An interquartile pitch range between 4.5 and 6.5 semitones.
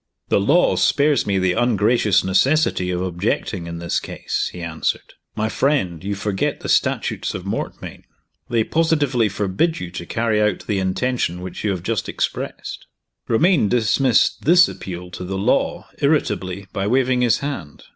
Yes: wide, 5.5 semitones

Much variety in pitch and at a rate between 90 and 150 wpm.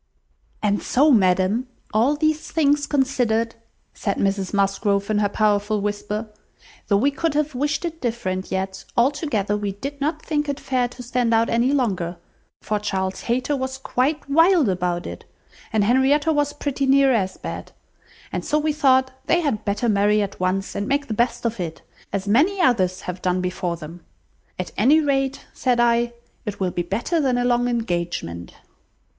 No: wide, 5.9 semitones; average, 175 wpm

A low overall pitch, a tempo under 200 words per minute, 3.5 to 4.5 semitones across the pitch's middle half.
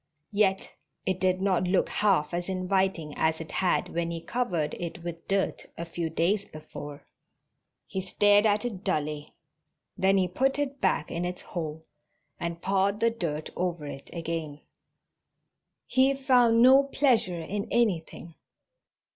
No: medium, 185 Hz; average, 145 wpm; average, 3.8 semitones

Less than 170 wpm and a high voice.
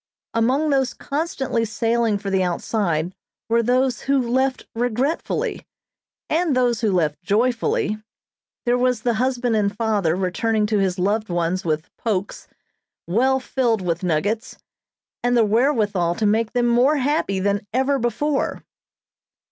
Yes: average, 140 wpm; high, 225 Hz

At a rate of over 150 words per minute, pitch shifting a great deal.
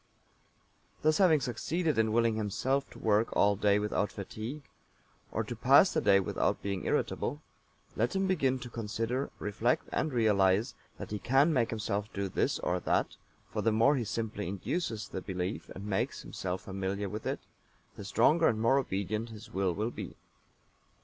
No: average, 170 wpm; average, 3.7 semitones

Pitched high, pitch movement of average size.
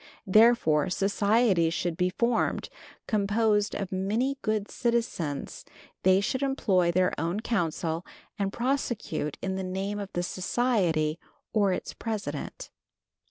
Yes: high, 195 Hz; average, 4.1 semitones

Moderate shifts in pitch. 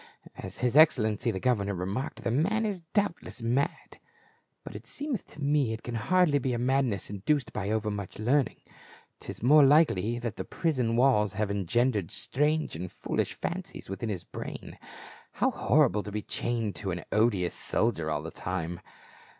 No: wide, 5.7 semitones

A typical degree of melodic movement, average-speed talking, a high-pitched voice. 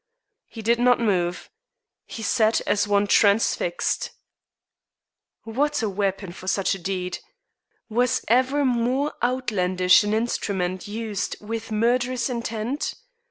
No: average, 3.6 semitones; slow, 115 wpm; high, 220 Hz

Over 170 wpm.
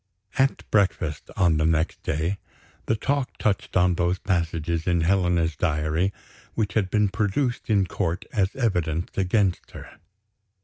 No: average, 140 wpm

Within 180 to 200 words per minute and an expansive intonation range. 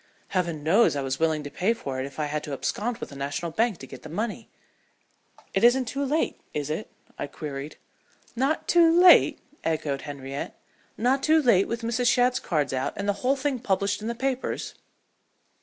Yes: average, 195 wpm; wide, 8.9 semitones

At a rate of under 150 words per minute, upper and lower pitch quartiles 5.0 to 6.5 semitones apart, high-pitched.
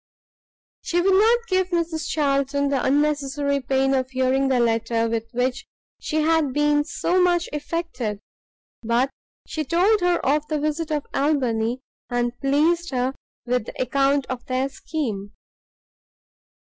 No: average, 140 wpm; average, 3.8 semitones; very high, 280 Hz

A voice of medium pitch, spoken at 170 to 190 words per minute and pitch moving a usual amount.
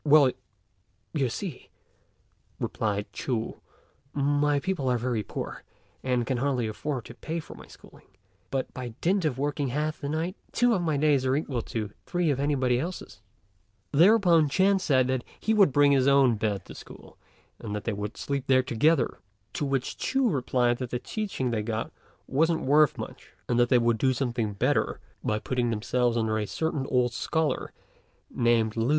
No: low, 130 Hz; average, 175 wpm; average, 4.2 semitones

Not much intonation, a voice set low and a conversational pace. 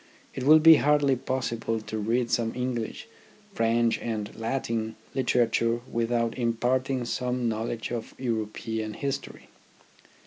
No: narrow, 2.0 semitones; low, 115 Hz; slow, 125 wpm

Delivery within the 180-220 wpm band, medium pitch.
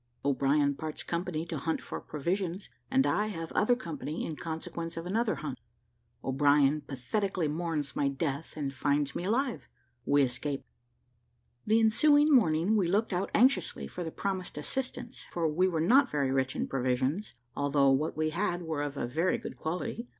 No: average, 170 wpm; medium, 165 Hz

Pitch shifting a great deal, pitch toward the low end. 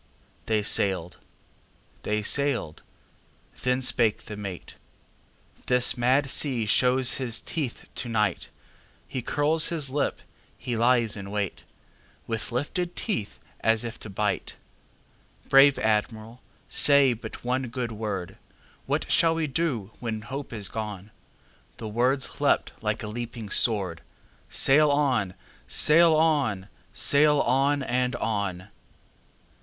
No: average, 4.5 semitones; low, 120 Hz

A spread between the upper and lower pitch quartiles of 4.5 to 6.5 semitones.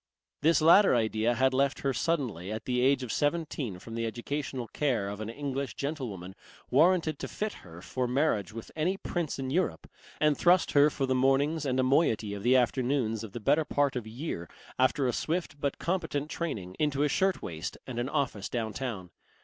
Yes: average, 4.8 semitones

